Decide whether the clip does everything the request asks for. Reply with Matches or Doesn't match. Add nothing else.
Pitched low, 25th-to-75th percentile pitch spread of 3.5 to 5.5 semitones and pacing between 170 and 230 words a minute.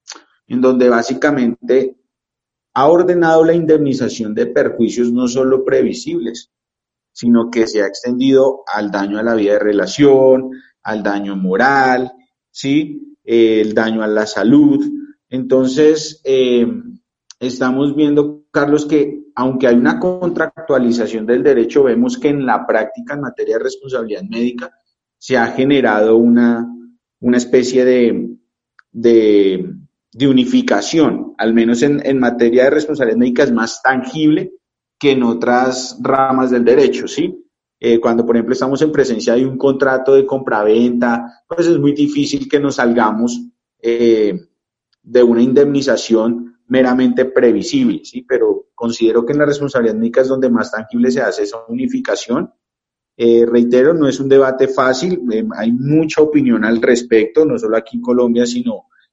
Doesn't match